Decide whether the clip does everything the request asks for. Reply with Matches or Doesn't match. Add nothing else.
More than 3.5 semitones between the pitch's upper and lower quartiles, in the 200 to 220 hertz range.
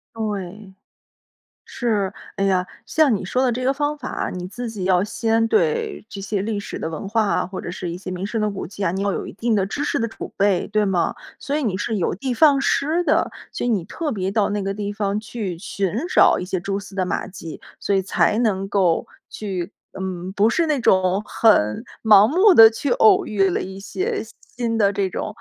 Doesn't match